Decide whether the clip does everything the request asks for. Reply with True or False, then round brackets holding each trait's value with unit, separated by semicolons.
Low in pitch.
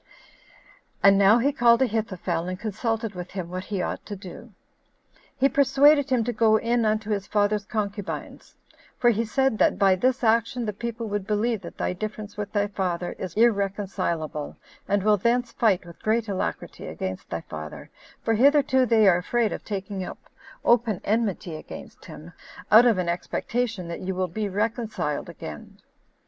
False (210 Hz)